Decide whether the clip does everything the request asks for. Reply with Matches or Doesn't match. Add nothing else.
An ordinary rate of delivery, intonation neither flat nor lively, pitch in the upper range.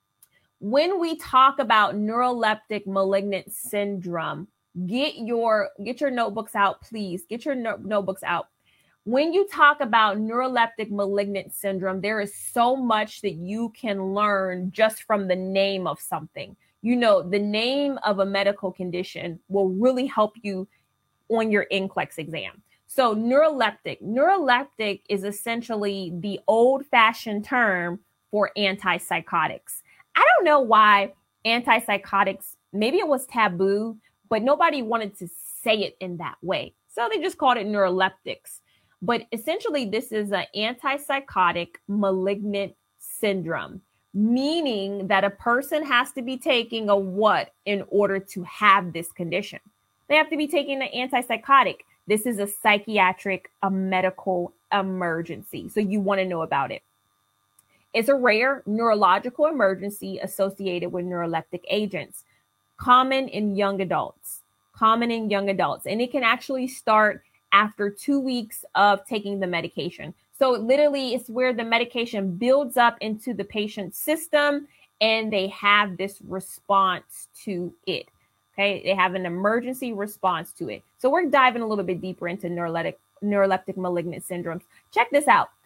Matches